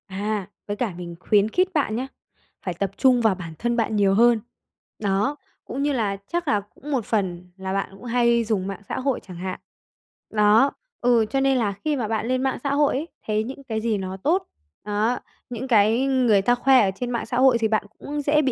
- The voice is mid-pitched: No, high, 225 Hz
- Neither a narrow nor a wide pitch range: Yes, average, 4.5 semitones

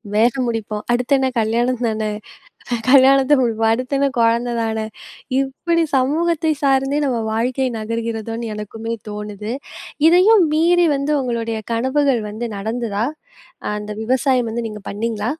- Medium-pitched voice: No, high, 240 Hz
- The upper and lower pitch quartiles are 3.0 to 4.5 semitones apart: Yes, average, 3.5 semitones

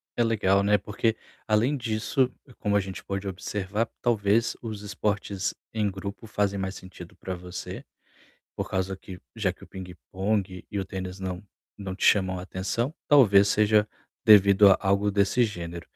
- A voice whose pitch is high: No, low, 100 Hz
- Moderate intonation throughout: No, narrow, 2.2 semitones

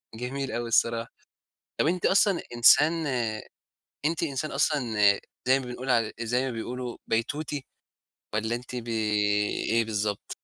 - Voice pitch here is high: No, low, 125 Hz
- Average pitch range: Yes, average, 3.4 semitones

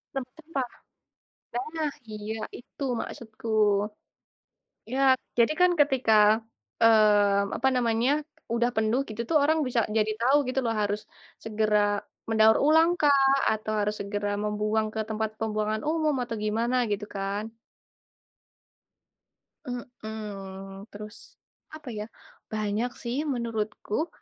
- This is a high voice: Yes, high, 220 Hz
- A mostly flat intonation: No, average, 3.1 semitones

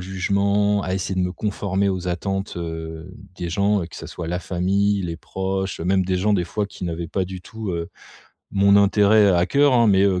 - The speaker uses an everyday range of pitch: No, narrow, 2.2 semitones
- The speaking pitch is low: Yes, very low, 95 Hz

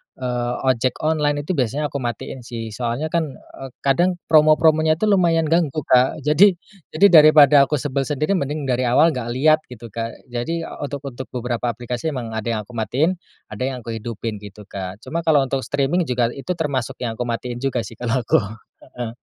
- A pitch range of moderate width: Yes, average, 4.3 semitones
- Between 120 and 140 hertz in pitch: Yes, low, 135 Hz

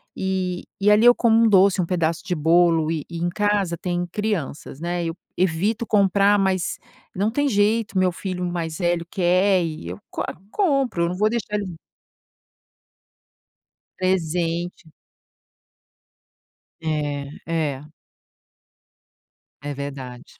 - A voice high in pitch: No, medium, 180 Hz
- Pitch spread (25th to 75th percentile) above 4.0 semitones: No, average, 3.7 semitones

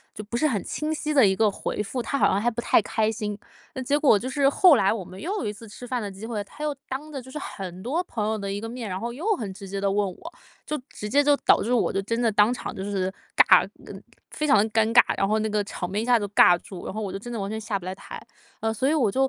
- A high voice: Yes, high, 220 Hz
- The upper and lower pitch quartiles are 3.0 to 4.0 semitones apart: No, average, 4.5 semitones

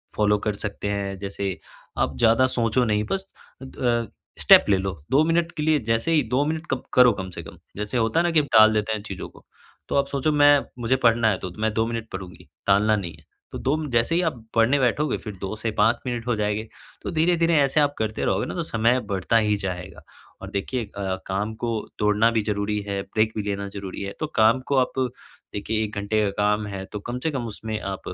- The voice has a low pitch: Yes, low, 110 Hz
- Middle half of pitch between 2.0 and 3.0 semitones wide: No, average, 4.1 semitones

